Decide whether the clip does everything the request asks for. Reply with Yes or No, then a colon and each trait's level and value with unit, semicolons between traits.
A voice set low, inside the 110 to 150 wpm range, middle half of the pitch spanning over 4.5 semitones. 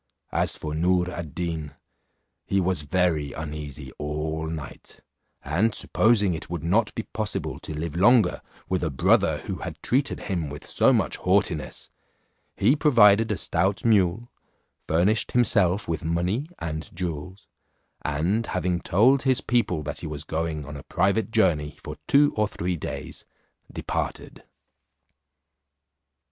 Yes: very low, 90 Hz; average, 140 wpm; average, 5.2 semitones